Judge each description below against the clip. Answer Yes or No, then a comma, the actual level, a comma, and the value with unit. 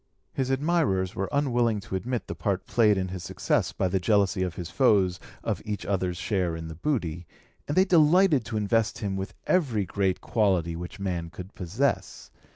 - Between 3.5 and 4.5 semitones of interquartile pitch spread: No, average, 5.0 semitones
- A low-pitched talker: Yes, low, 100 Hz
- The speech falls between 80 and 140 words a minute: No, average, 185 wpm